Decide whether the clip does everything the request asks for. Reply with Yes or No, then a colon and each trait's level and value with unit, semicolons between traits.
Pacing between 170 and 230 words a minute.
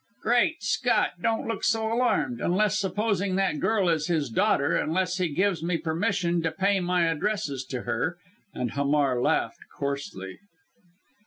No: average, 150 wpm